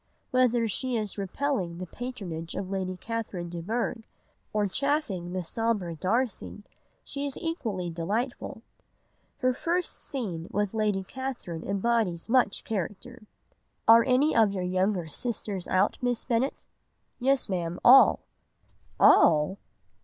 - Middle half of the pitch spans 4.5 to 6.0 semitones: Yes, average, 5.1 semitones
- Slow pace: Yes, slow, 125 wpm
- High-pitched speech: Yes, high, 215 Hz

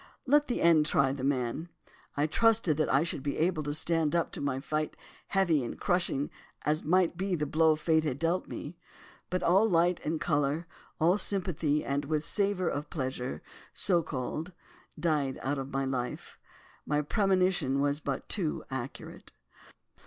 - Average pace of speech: Yes, average, 165 wpm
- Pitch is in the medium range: Yes, medium, 155 Hz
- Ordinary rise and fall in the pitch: Yes, average, 3.7 semitones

